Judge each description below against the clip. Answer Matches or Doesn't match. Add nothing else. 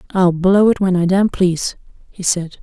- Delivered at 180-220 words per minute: Matches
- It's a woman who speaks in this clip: Matches